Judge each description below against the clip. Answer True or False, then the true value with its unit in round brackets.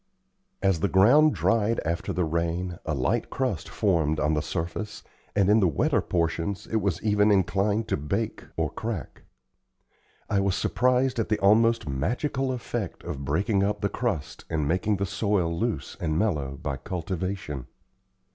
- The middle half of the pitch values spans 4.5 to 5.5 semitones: True (4.8 semitones)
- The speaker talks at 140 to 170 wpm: True (160 wpm)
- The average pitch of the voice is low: True (95 Hz)